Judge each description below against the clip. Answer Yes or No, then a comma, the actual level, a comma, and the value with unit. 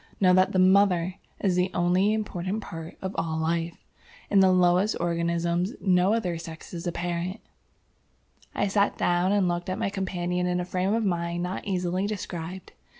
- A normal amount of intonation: No, narrow, 1.8 semitones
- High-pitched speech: No, medium, 180 Hz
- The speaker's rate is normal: Yes, average, 170 wpm